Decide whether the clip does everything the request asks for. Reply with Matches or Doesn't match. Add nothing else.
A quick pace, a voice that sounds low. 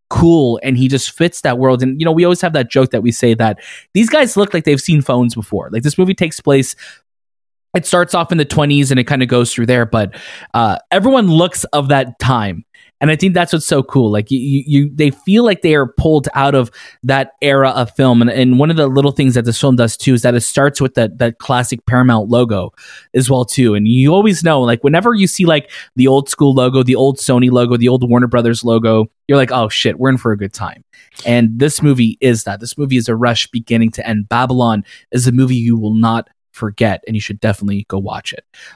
Matches